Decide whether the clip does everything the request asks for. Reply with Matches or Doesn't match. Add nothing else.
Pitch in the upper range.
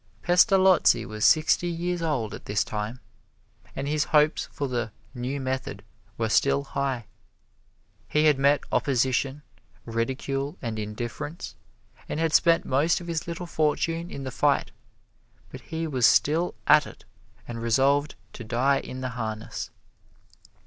Doesn't match